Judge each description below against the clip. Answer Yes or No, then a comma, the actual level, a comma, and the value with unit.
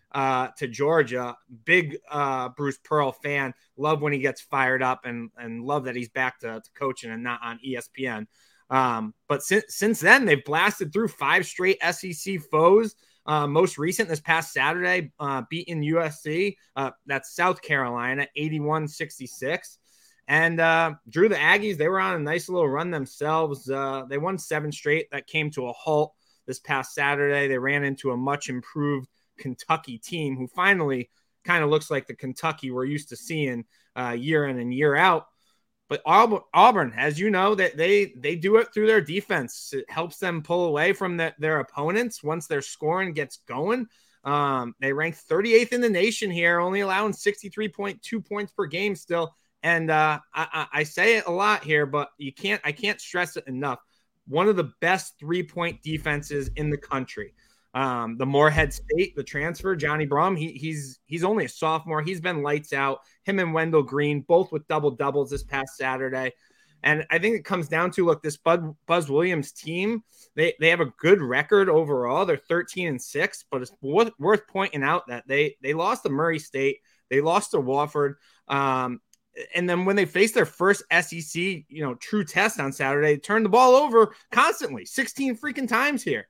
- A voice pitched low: No, medium, 155 Hz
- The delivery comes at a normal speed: Yes, average, 185 wpm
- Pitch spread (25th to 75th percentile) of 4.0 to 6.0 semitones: Yes, average, 5.0 semitones